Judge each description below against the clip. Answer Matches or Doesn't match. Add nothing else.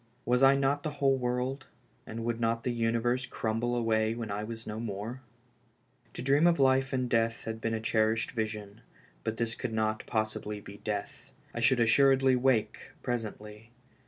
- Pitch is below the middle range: Matches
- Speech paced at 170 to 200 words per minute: Matches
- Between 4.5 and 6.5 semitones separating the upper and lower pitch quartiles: Doesn't match